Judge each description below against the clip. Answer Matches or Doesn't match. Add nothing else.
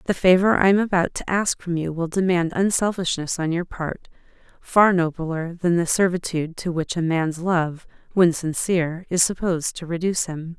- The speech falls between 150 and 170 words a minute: Doesn't match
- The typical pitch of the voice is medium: Matches